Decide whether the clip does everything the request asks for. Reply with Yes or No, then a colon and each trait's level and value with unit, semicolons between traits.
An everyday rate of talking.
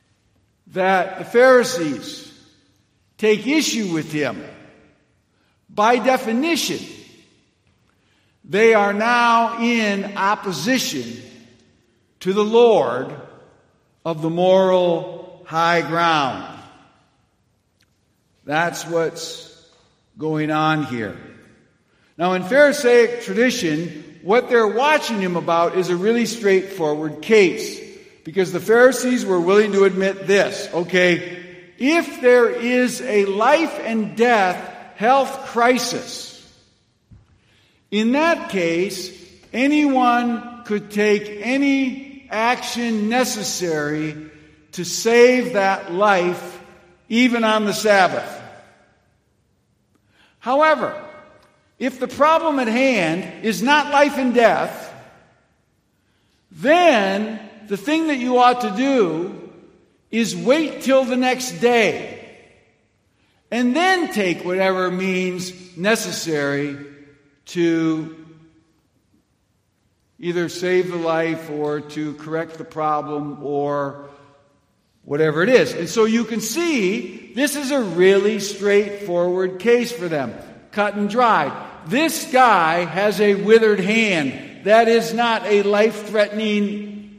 No: slow, 105 wpm